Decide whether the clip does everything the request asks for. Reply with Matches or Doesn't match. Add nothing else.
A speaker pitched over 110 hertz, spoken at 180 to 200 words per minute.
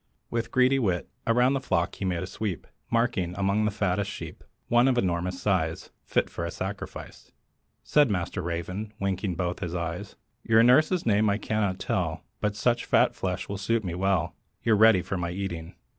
Doesn't match